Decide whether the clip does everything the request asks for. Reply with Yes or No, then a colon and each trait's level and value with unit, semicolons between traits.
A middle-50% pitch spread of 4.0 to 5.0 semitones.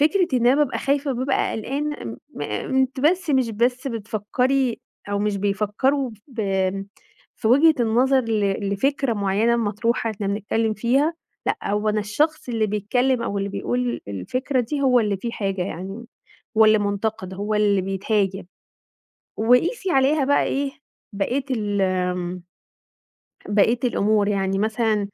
Yes: average, 4.4 semitones